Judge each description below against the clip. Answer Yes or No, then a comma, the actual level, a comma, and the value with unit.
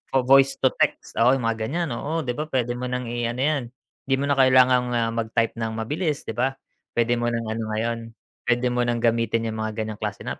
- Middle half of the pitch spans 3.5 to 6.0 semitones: No, narrow, 2.5 semitones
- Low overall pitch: Yes, low, 120 Hz